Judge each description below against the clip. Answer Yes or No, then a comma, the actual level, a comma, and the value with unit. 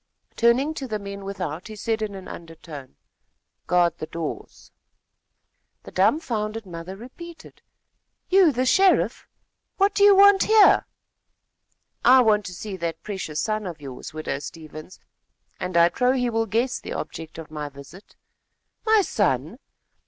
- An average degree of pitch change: No, wide, 7.3 semitones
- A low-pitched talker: No, high, 205 Hz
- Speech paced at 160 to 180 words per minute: No, average, 145 wpm